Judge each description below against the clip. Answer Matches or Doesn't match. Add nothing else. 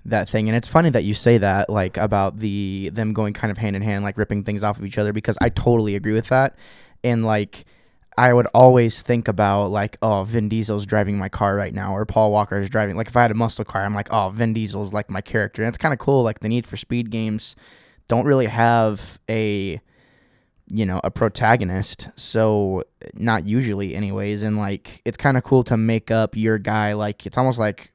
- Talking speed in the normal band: Doesn't match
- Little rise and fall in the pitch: Matches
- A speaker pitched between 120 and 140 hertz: Doesn't match